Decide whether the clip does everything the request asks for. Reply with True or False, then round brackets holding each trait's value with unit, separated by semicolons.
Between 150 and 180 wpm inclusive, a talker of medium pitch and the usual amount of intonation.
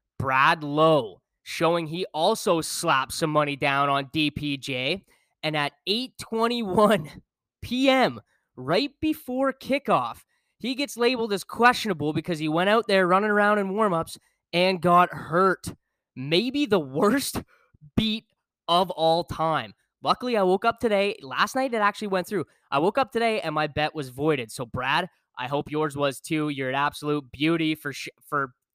False (160 wpm; 170 Hz; 6.3 semitones)